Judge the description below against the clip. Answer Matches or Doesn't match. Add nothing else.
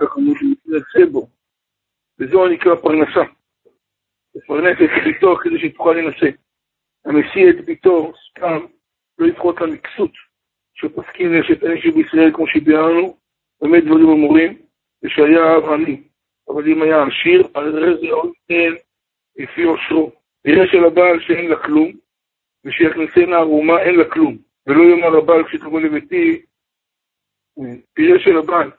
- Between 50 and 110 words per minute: Doesn't match